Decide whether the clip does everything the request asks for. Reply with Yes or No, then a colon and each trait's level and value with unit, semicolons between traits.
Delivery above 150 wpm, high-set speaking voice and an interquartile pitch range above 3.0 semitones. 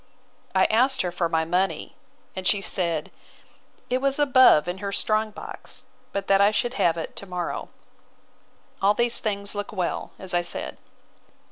Yes: average, 165 wpm; high, 195 Hz; average, 3.5 semitones